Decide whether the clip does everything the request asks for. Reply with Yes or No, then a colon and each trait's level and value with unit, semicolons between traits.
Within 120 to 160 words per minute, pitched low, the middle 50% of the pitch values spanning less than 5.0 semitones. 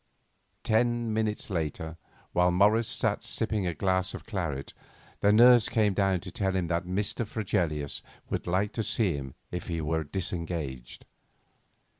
Yes: average, 150 wpm; very low, 95 Hz; average, 4.2 semitones